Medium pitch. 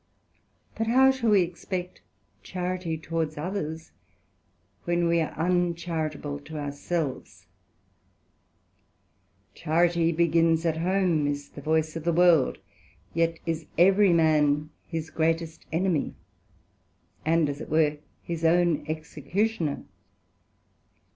Yes: medium, 165 Hz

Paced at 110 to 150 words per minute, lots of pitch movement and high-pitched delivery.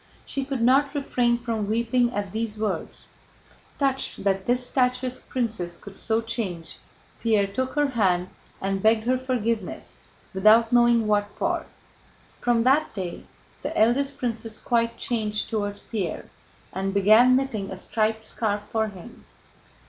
No: average, 140 wpm; average, 3.3 semitones; high, 225 Hz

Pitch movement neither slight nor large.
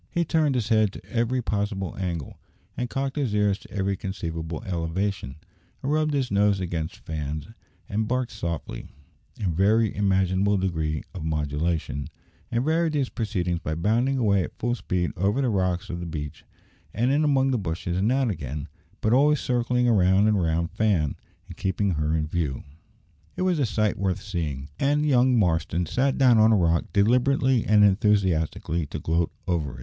No: wide, 6.3 semitones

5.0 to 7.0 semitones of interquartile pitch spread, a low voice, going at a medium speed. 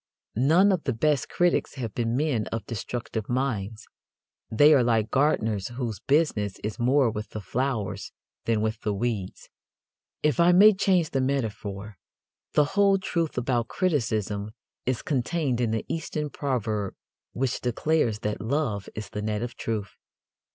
Yes: wide, 5.5 semitones; low, 120 Hz; average, 150 wpm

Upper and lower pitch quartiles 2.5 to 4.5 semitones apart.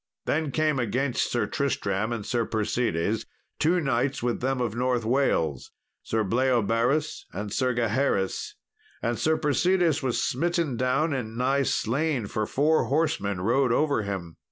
Yes: average, 4.2 semitones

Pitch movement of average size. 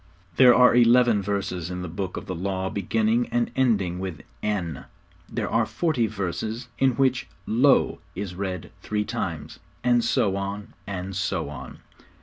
Yes: average, 4.4 semitones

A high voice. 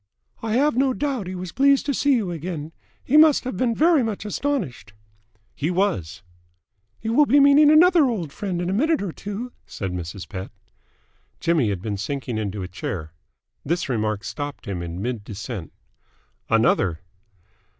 No: medium, 180 Hz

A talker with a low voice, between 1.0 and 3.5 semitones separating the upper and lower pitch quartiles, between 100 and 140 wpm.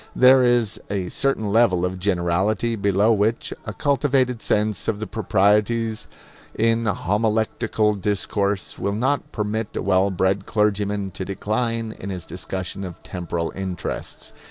Yes: low, 105 Hz; average, 2.9 semitones; slow, 135 wpm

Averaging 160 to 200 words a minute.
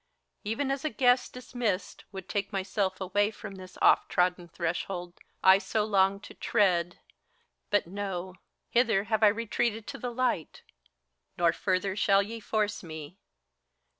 No: average, 145 wpm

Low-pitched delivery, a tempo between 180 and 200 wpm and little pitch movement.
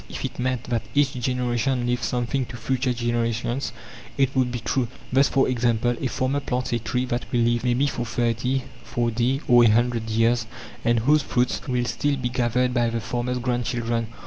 Yes: low, 120 Hz; average, 190 wpm; narrow, 1.4 semitones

